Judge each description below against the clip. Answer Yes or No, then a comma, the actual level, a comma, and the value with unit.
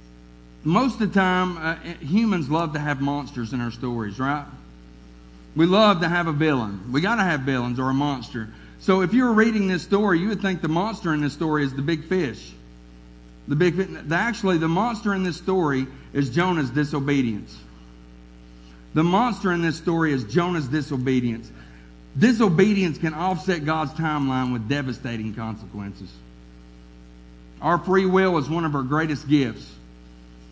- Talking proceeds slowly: No, average, 165 wpm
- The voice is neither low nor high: Yes, medium, 145 Hz